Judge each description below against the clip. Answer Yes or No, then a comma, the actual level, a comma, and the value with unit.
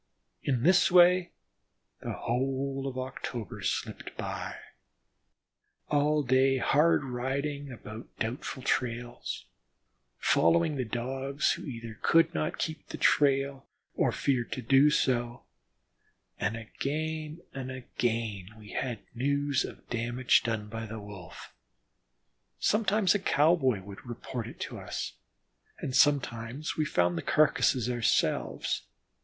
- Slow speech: Yes, slow, 125 wpm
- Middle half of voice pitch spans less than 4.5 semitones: Yes, average, 3.8 semitones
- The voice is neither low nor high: No, low, 130 Hz